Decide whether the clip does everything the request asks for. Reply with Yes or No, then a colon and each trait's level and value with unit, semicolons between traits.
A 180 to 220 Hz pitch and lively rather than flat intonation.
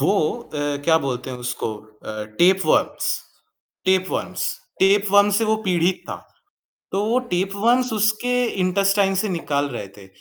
Yes: high, 190 Hz; wide, 6.3 semitones